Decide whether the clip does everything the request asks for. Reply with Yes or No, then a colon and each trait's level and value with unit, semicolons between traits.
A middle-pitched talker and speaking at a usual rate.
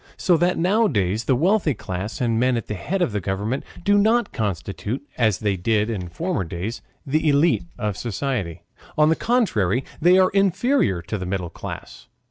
No: low, 120 Hz; average, 175 wpm